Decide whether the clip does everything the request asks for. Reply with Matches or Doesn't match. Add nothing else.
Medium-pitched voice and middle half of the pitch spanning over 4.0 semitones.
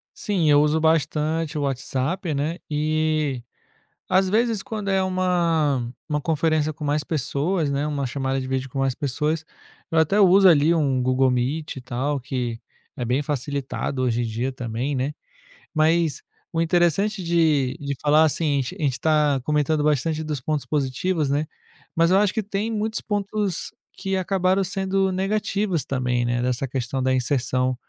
Matches